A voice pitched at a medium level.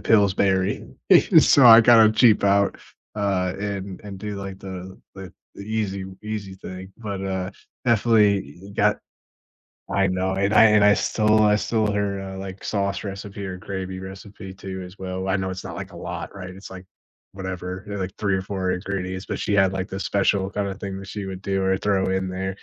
No: very low, 95 Hz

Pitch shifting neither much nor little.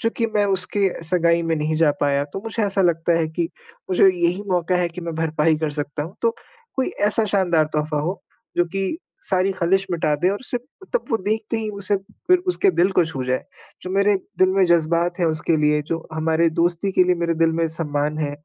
Yes: average, 3.4 semitones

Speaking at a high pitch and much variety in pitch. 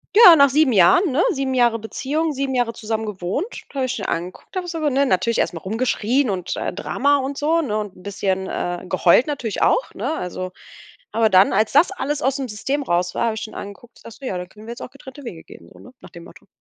Yes: high, 235 Hz; wide, 6.1 semitones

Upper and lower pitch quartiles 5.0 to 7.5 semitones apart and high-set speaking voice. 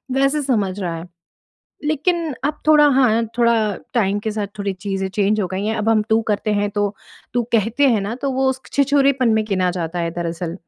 Yes: average, 5.3 semitones; high, 215 Hz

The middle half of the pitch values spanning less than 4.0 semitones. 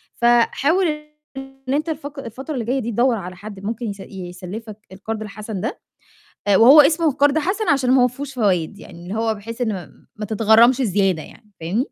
No: average, 4.9 semitones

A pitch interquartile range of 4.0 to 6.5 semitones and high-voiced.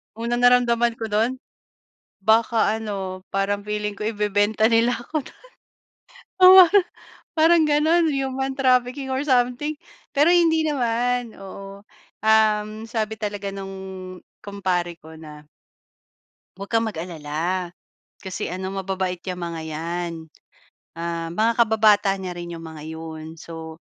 Yes: average, 5.0 semitones; high, 210 Hz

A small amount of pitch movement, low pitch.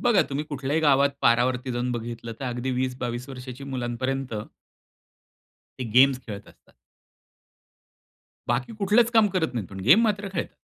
No: average, 3.3 semitones; low, 130 Hz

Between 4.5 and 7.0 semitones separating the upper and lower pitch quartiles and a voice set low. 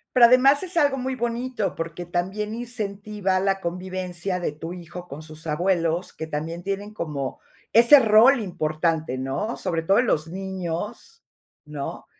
No: average, 5.2 semitones; medium, 185 Hz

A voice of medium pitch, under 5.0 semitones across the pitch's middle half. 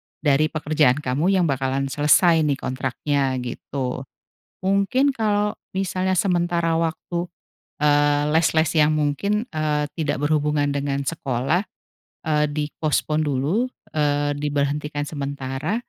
Yes: medium, 150 Hz; average, 2.8 semitones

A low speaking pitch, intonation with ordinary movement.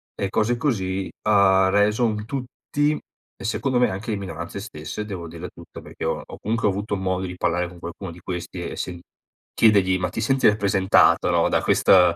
Yes: low, 100 Hz; average, 3.1 semitones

